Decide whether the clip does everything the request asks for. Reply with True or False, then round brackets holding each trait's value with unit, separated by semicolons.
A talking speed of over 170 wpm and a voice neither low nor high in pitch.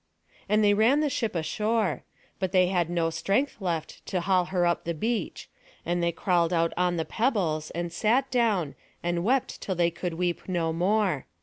True (190 wpm; 180 Hz)